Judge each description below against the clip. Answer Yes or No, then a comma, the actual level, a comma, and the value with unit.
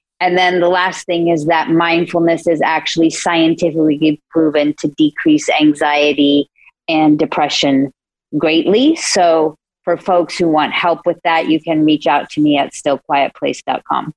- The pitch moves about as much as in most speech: No, narrow, 2.3 semitones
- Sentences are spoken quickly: No, average, 145 wpm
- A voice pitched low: No, medium, 160 Hz